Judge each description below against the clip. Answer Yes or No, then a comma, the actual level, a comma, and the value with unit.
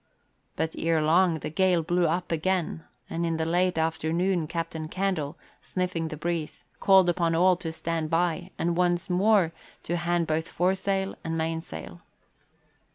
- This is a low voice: No, medium, 170 Hz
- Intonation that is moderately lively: No, narrow, 1.9 semitones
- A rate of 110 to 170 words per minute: Yes, average, 155 wpm